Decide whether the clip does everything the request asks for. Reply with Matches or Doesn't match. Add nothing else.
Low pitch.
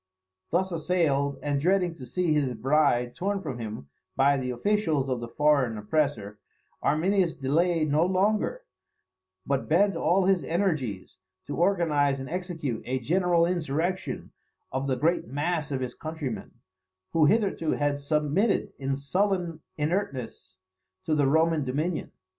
Doesn't match